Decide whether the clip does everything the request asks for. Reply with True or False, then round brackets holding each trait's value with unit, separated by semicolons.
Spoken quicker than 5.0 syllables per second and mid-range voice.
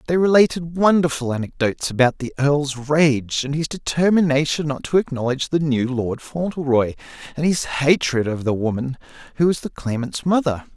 True (5.2 syllables/s; 145 Hz)